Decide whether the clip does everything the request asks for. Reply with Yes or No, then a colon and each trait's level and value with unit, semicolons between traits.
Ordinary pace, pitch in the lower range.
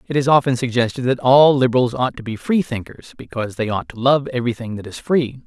No: fast, 220 wpm; low, 125 Hz